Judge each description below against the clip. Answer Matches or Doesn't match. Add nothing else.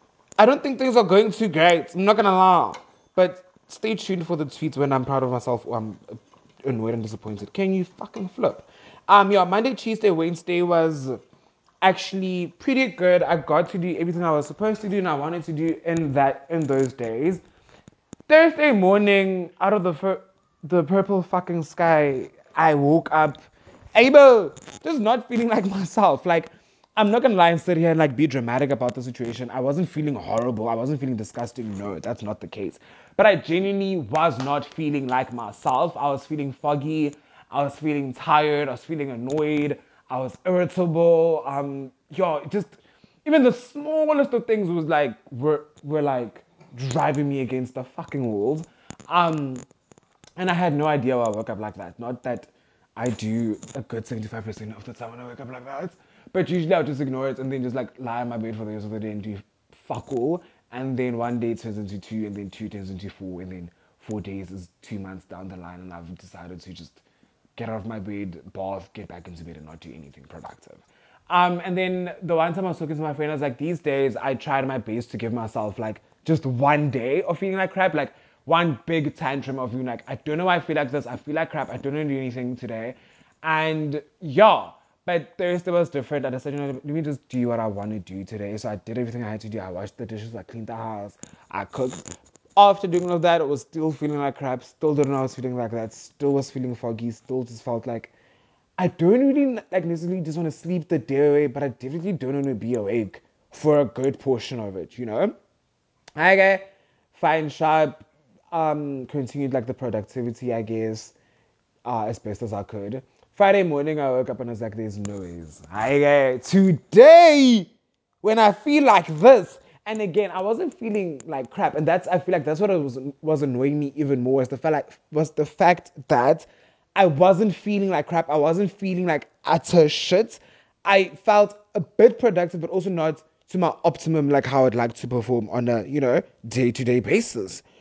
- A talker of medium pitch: Matches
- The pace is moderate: Doesn't match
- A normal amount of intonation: Doesn't match